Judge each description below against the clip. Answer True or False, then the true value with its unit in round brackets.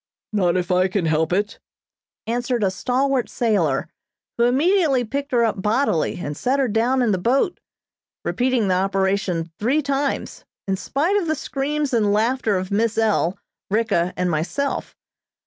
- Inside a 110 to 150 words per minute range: False (160 wpm)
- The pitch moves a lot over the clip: True (6.0 semitones)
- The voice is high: True (225 Hz)